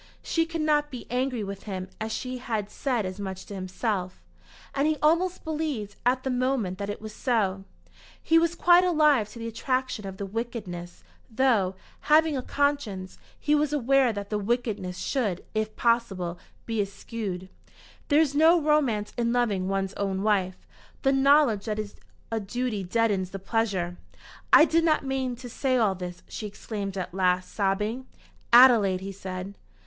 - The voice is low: No, high, 225 Hz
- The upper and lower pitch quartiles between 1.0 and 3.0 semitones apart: No, wide, 5.5 semitones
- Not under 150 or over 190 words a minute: Yes, average, 175 wpm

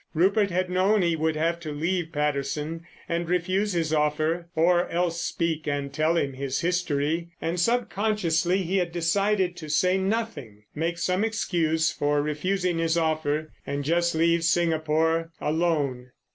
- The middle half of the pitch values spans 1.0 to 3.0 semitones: Yes, narrow, 2.6 semitones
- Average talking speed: Yes, average, 150 wpm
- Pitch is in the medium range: Yes, medium, 165 Hz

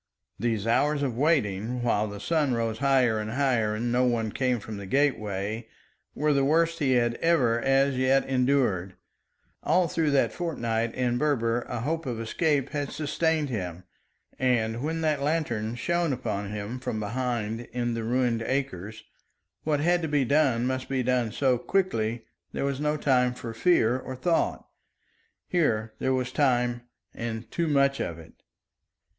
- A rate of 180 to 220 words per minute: No, average, 165 wpm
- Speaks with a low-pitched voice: Yes, low, 125 Hz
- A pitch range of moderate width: Yes, average, 4.0 semitones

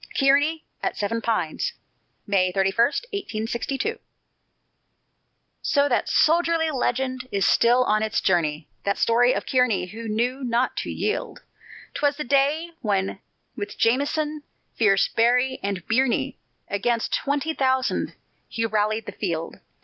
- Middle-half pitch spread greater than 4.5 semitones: Yes, average, 4.9 semitones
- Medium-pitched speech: No, high, 240 Hz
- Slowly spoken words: Yes, slow, 125 wpm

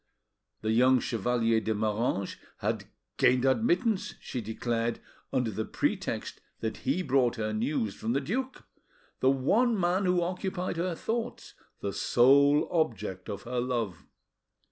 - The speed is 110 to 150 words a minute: Yes, average, 140 wpm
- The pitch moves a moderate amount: No, wide, 7.7 semitones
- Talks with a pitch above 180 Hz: No, low, 125 Hz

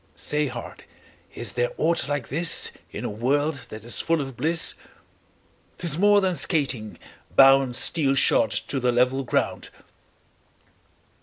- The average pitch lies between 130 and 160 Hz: Yes, medium, 140 Hz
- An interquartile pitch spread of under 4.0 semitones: No, average, 4.6 semitones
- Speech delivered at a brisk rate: No, average, 145 wpm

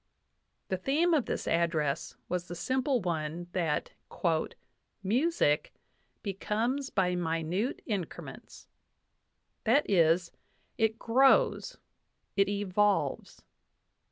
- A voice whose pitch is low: No, high, 195 Hz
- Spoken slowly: Yes, slow, 95 wpm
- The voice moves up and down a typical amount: No, wide, 5.7 semitones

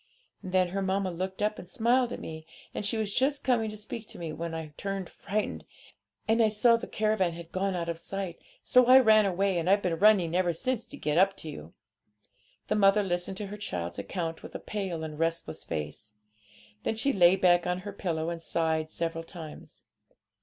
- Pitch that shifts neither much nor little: Yes, average, 4.1 semitones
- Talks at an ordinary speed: No, fast, 210 wpm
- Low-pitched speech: No, medium, 185 Hz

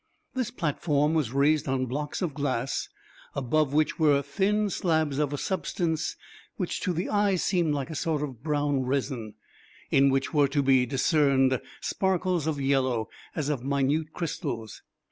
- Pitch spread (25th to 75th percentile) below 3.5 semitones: Yes, average, 3.1 semitones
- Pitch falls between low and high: Yes, medium, 145 Hz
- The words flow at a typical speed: Yes, average, 160 wpm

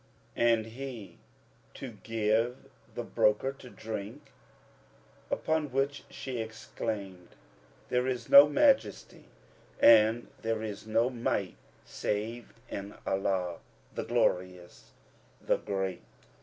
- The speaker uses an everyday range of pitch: Yes, average, 3.7 semitones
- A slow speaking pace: Yes, slow, 100 wpm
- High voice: No, low, 110 Hz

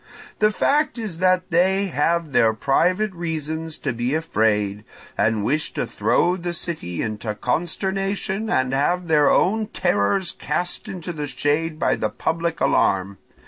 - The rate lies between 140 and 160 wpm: Yes, average, 145 wpm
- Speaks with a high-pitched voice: No, medium, 165 Hz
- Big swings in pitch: Yes, wide, 6.2 semitones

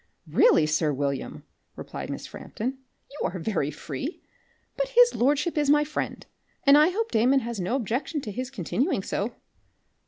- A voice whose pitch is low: No, very high, 260 Hz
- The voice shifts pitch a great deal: Yes, wide, 6.9 semitones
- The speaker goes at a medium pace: Yes, average, 160 wpm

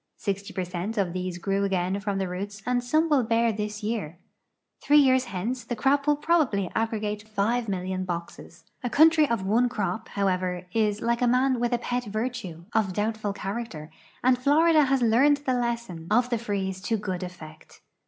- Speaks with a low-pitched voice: No, high, 215 Hz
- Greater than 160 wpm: Yes, average, 185 wpm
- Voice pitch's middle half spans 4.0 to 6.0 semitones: Yes, average, 4.4 semitones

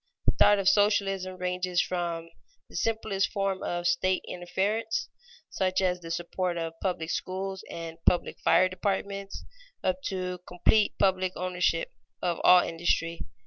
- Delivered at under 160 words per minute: Yes, average, 140 wpm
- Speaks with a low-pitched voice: No, medium, 185 Hz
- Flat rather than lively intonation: Yes, narrow, 1.9 semitones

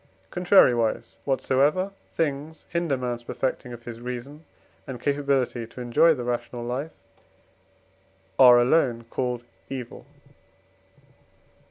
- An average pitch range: Yes, average, 3.2 semitones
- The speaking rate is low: Yes, slow, 105 wpm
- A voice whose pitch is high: No, low, 130 Hz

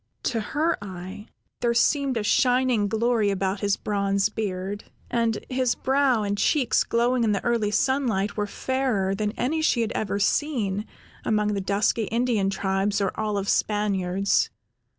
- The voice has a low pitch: No, high, 210 Hz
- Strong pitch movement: No, average, 3.5 semitones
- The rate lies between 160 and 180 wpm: No, average, 150 wpm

